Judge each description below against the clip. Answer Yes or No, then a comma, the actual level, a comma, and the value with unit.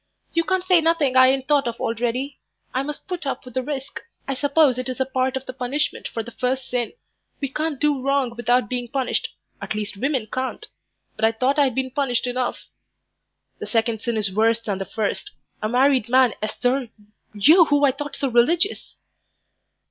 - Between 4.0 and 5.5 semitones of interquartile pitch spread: No, average, 3.0 semitones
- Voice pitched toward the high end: Yes, very high, 260 Hz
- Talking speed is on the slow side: No, average, 195 wpm